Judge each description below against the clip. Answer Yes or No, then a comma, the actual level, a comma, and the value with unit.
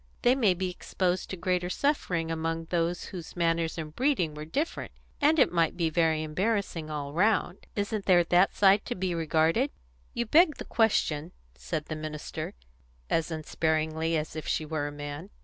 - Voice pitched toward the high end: No, medium, 170 Hz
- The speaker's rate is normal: Yes, average, 175 wpm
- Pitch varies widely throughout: No, average, 3.5 semitones